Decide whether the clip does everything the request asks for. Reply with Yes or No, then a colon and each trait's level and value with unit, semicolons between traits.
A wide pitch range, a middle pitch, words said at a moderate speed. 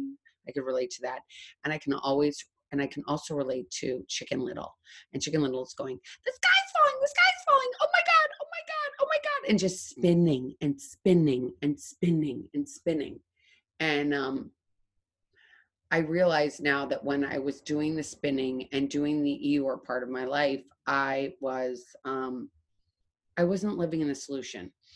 Yes: wide, 5.9 semitones; medium, 145 Hz; average, 180 wpm